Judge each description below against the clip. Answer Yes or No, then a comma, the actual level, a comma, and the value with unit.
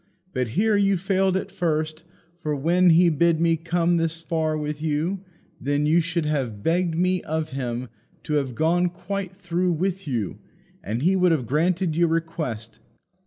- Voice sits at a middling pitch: Yes, medium, 165 Hz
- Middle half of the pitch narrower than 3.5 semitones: Yes, average, 3.0 semitones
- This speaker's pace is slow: No, average, 170 wpm